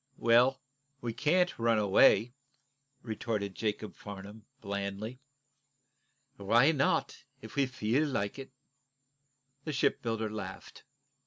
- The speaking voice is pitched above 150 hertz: No, low, 115 Hz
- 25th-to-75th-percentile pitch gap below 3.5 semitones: No, average, 4.3 semitones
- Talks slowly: Yes, slow, 100 wpm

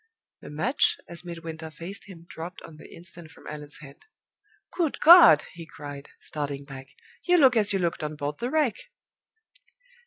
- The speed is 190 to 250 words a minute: No, average, 165 wpm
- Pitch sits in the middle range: Yes, medium, 165 Hz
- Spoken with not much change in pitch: No, average, 5.3 semitones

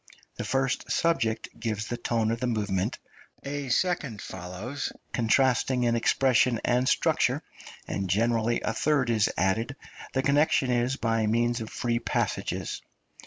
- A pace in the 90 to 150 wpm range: Yes, average, 140 wpm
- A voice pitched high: No, low, 120 Hz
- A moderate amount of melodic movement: Yes, average, 3.0 semitones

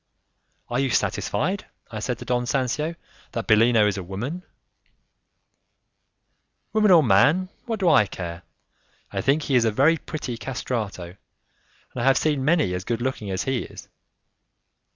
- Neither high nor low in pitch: No, low, 125 Hz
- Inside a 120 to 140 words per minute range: No, average, 155 wpm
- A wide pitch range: Yes, wide, 6.0 semitones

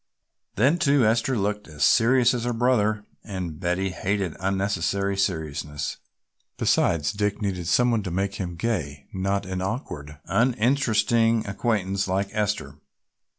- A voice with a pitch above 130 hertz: No, low, 100 Hz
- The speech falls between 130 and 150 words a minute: Yes, slow, 135 wpm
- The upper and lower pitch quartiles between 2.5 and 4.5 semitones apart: Yes, average, 3.6 semitones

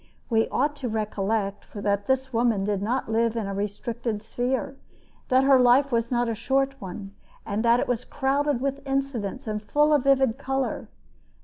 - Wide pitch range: No, average, 4.0 semitones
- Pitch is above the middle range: Yes, high, 240 Hz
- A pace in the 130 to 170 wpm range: No, average, 180 wpm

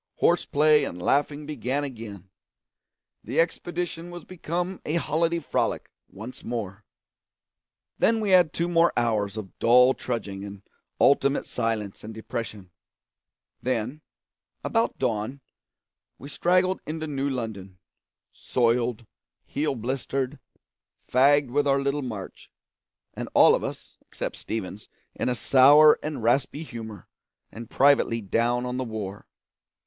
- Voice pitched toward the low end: Yes, low, 130 Hz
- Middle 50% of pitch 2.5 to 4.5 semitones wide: No, average, 5.1 semitones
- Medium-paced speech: No, slow, 125 wpm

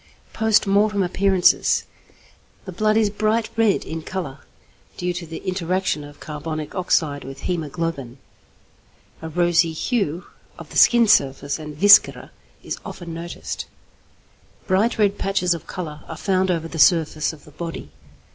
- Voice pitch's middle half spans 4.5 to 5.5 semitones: No, average, 4.0 semitones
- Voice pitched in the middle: Yes, medium, 175 Hz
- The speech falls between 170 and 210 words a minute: No, average, 145 wpm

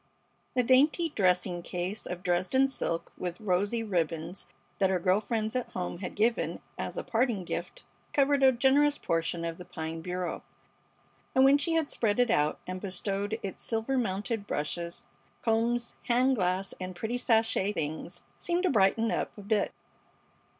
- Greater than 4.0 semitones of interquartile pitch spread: Yes, average, 5.2 semitones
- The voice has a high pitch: Yes, high, 205 Hz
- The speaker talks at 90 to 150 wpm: No, average, 165 wpm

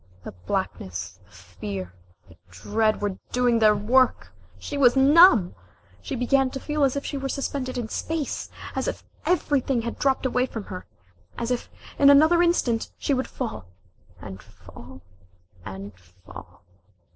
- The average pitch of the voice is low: No, high, 240 Hz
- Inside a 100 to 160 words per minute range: Yes, average, 155 wpm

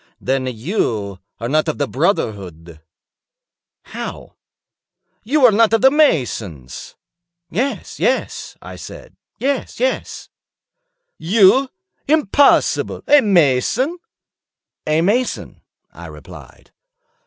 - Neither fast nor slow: No, slow, 95 wpm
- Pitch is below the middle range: No, medium, 175 Hz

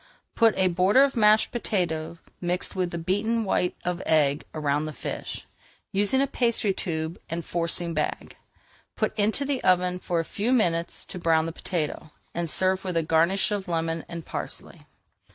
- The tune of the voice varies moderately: Yes, average, 3.8 semitones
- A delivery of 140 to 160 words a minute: No, average, 170 wpm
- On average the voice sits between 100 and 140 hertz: No, medium, 180 Hz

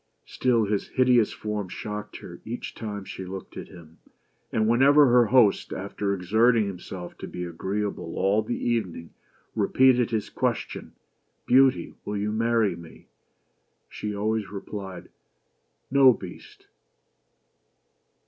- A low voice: Yes, low, 105 Hz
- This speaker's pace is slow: Yes, slow, 130 wpm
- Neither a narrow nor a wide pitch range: Yes, average, 3.5 semitones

